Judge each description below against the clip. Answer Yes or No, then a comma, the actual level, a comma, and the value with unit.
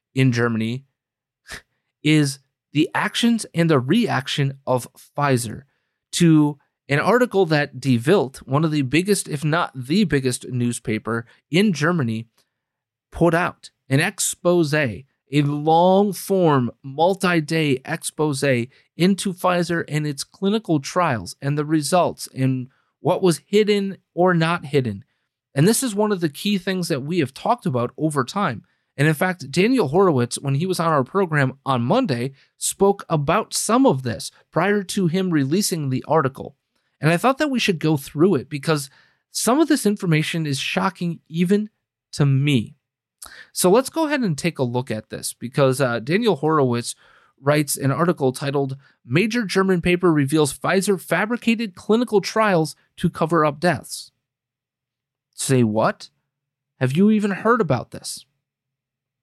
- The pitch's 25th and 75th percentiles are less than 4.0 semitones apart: No, average, 5.3 semitones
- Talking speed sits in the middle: Yes, average, 150 wpm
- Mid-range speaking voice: Yes, medium, 155 Hz